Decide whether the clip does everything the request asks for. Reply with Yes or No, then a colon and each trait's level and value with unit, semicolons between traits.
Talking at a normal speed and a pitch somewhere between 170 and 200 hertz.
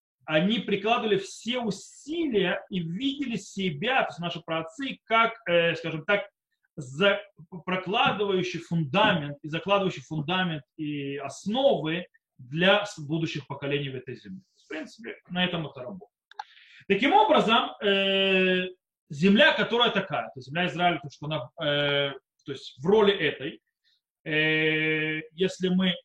Yes: average, 130 wpm; medium, 185 Hz